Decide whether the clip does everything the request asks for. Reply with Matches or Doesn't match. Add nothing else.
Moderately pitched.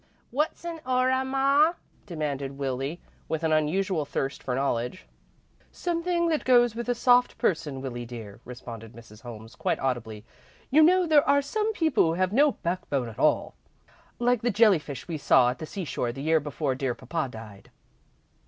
Matches